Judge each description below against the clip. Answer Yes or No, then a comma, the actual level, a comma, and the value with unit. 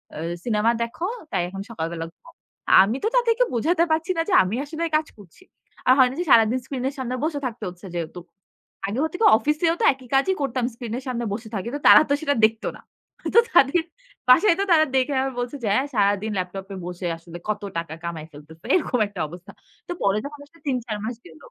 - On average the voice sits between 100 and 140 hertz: No, high, 240 Hz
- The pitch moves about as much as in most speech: No, wide, 7.1 semitones